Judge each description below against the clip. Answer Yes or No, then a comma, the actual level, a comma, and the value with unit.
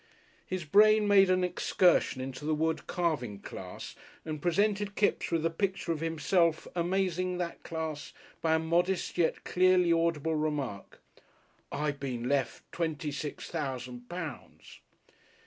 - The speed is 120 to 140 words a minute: Yes, slow, 135 wpm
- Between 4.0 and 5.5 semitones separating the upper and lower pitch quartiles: No, average, 3.4 semitones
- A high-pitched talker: No, medium, 165 Hz